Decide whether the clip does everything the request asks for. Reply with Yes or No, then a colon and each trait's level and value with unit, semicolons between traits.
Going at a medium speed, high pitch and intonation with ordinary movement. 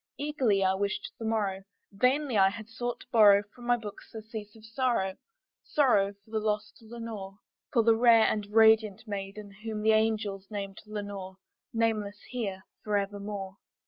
No: average, 155 wpm; high, 215 Hz; narrow, 2.2 semitones